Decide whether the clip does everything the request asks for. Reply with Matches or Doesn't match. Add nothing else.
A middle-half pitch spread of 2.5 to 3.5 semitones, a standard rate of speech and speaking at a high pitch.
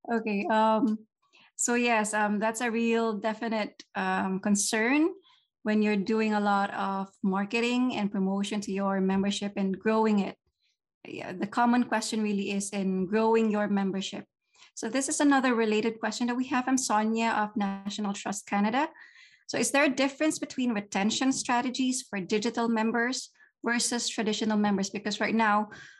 Matches